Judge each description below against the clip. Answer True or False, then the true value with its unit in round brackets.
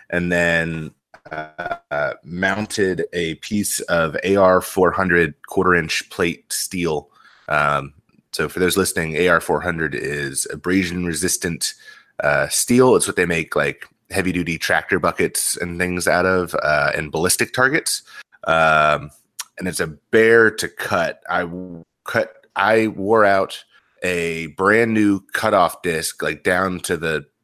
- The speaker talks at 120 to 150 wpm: True (140 wpm)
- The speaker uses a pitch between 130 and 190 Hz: False (90 Hz)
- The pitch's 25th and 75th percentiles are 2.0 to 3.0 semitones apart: True (2.6 semitones)